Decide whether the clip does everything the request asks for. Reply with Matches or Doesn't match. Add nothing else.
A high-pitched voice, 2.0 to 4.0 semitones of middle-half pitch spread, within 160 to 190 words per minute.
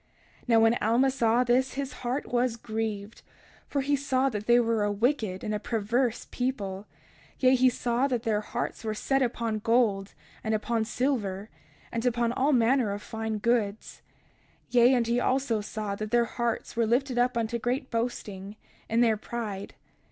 Matches